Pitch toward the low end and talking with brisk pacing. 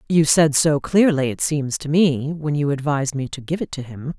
No: medium, 145 Hz; fast, 245 wpm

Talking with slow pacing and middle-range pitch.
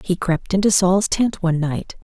No: average, 200 wpm; medium, 180 Hz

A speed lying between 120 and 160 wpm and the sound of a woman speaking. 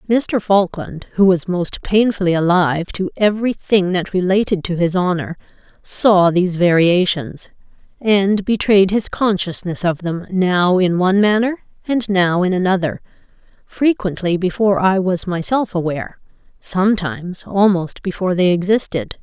Yes: slow, 135 wpm; female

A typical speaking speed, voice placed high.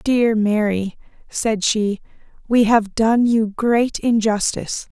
No: slow, 120 wpm; high, 220 Hz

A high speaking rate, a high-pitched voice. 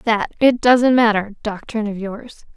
No: average, 165 wpm; high, 220 Hz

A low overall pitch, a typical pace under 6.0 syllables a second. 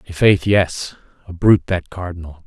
Yes: very low, 90 Hz; 5.2 syllables/s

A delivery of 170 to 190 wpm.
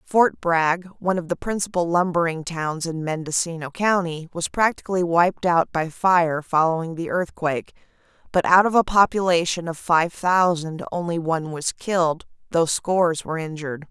No: average, 155 wpm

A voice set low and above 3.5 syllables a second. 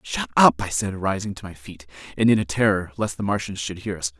Yes: very low, 95 Hz; 5.8 syllables/s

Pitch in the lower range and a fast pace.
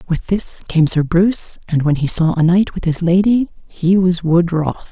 No: medium, 175 Hz; fast, 220 wpm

